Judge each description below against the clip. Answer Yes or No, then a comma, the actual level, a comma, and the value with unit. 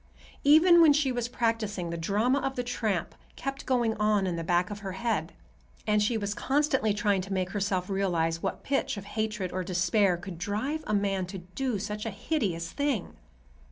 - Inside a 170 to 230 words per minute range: Yes, average, 195 wpm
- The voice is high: Yes, high, 205 Hz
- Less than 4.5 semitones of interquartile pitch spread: No, average, 4.8 semitones